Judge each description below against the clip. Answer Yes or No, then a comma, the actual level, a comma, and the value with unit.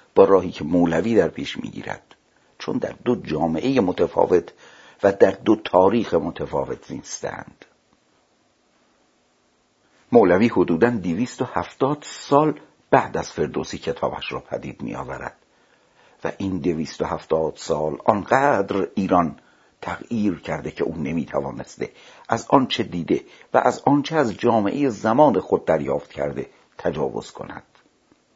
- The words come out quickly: No, average, 125 wpm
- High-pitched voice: No, medium, 140 Hz